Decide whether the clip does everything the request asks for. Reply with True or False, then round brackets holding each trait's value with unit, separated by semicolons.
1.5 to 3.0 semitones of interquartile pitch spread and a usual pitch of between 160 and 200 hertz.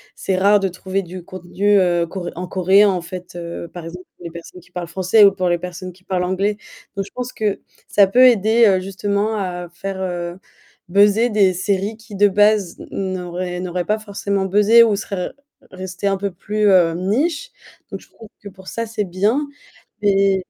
True (2.4 semitones; 190 Hz)